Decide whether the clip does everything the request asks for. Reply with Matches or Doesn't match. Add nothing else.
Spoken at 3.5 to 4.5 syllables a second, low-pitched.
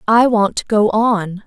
Doesn't match